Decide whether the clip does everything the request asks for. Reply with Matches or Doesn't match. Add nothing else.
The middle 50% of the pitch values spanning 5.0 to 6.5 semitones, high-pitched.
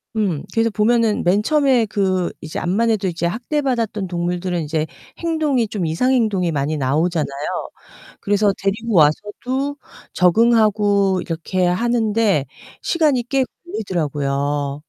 Matches